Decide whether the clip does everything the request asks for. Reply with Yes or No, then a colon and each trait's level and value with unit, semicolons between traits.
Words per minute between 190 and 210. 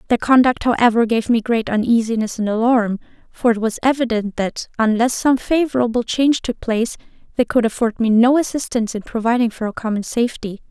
No: average, 180 wpm